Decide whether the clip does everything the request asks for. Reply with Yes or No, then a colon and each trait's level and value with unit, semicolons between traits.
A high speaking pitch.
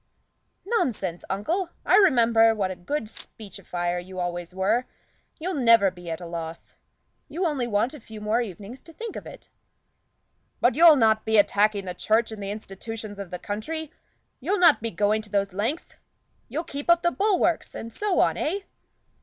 Yes: high, 220 Hz